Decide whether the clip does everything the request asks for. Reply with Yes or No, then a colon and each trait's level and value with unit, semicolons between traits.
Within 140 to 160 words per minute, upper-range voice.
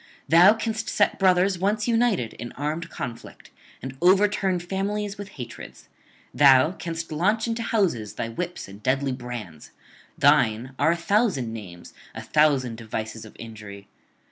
No: average, 145 wpm; medium, 155 Hz